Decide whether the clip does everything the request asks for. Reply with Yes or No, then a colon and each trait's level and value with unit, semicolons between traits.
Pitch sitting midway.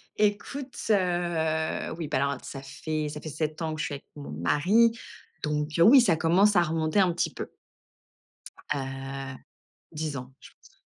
Yes: medium, 155 Hz